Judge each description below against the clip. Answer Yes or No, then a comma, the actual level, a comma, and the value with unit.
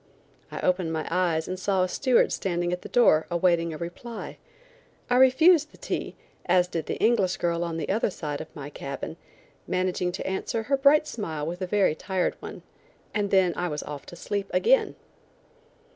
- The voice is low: No, medium, 180 Hz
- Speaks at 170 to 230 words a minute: Yes, average, 190 wpm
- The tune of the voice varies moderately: Yes, average, 3.9 semitones